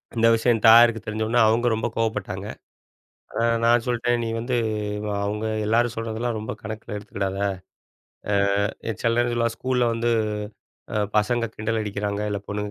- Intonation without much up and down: Yes, narrow, 1.8 semitones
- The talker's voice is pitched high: No, low, 115 Hz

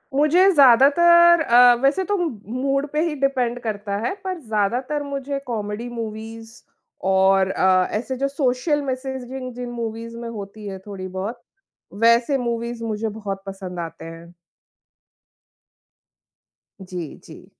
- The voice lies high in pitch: Yes, high, 235 Hz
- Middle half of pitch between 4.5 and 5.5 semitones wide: Yes, average, 4.8 semitones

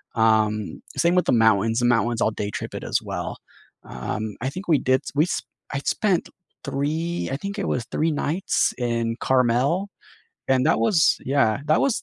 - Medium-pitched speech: No, low, 130 Hz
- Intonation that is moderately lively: No, wide, 6.2 semitones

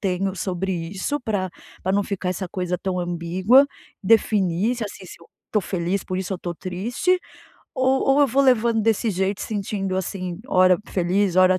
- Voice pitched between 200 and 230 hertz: No, high, 190 Hz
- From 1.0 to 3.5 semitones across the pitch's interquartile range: Yes, average, 2.9 semitones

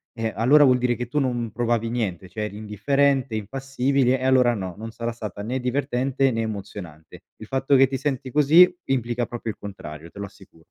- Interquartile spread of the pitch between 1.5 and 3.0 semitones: No, average, 3.9 semitones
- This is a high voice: No, low, 120 Hz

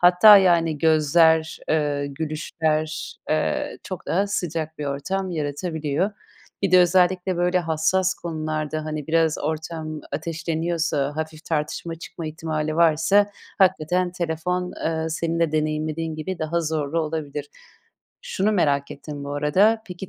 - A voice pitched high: No, medium, 160 Hz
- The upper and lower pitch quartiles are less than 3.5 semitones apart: Yes, narrow, 2.4 semitones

